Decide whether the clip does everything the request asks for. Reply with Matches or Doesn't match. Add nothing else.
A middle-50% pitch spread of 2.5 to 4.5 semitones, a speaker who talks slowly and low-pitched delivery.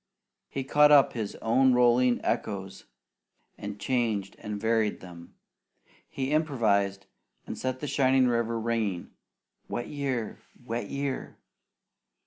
Matches